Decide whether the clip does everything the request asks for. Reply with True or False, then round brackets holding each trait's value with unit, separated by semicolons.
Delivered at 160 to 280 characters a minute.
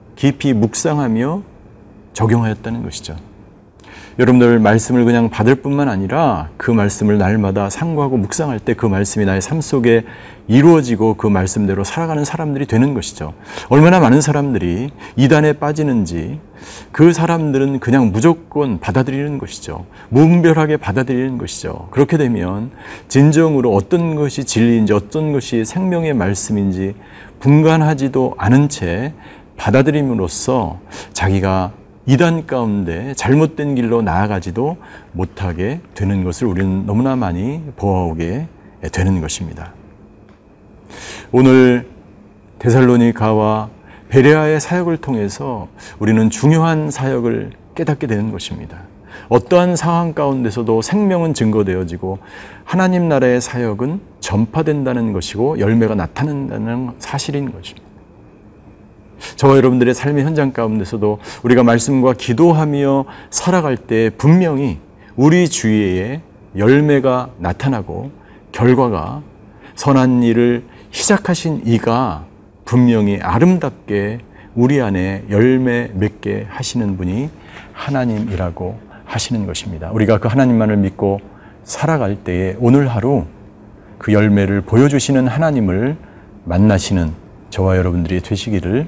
False (295 characters per minute)